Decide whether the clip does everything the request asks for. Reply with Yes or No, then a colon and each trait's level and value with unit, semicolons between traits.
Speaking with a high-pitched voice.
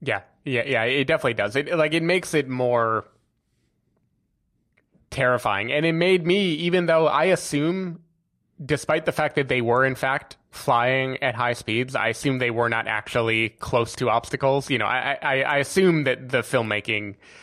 No: low, 135 Hz